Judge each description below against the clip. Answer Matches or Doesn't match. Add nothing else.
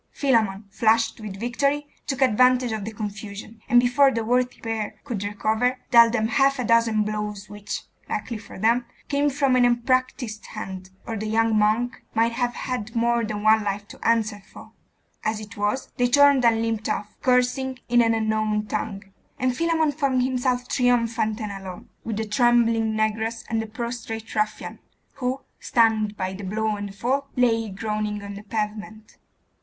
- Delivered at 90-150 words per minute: Doesn't match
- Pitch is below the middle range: Doesn't match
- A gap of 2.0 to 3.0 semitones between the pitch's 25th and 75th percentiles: Matches